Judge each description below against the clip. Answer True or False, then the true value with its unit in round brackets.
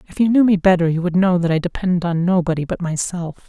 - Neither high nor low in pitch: True (175 Hz)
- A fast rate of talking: True (260 wpm)